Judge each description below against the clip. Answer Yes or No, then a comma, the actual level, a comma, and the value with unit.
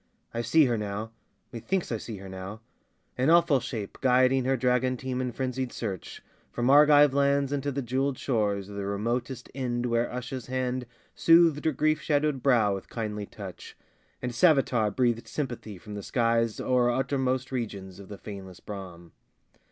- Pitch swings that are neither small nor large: Yes, average, 3.9 semitones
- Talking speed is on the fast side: No, average, 165 wpm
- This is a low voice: Yes, low, 125 Hz